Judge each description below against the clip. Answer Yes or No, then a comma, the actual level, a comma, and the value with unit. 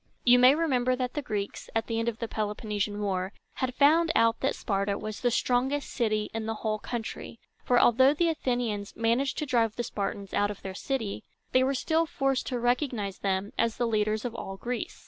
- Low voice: No, high, 230 Hz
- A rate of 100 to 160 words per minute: No, fast, 205 wpm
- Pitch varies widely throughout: No, average, 3.5 semitones